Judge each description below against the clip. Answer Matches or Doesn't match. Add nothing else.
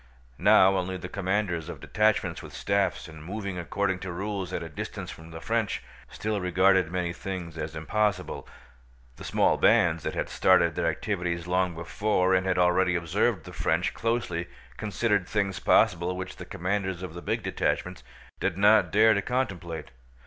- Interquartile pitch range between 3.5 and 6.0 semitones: Doesn't match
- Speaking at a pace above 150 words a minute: Matches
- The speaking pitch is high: Doesn't match